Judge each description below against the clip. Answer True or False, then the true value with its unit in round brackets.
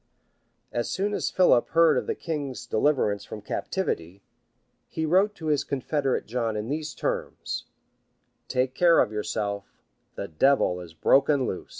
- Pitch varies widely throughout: True (6.9 semitones)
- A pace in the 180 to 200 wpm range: False (155 wpm)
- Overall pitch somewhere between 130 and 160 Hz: True (135 Hz)